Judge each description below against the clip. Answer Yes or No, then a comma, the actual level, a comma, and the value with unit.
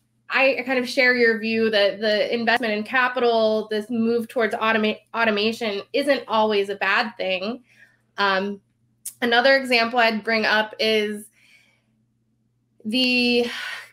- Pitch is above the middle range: Yes, high, 220 Hz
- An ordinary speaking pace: No, slow, 125 wpm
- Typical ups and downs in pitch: Yes, average, 3.0 semitones